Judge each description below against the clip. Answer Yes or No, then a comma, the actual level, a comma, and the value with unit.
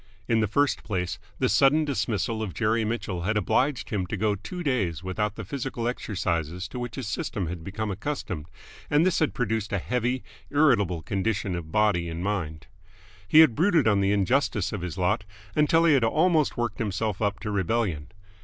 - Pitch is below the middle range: Yes, low, 105 Hz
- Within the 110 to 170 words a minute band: No, average, 190 wpm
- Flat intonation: No, average, 5.0 semitones